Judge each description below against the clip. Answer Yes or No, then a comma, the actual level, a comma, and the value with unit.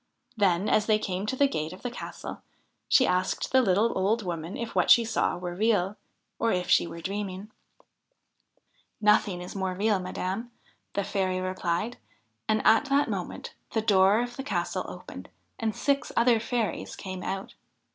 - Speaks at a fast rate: No, average, 175 wpm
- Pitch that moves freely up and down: No, average, 3.6 semitones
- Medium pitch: No, high, 205 Hz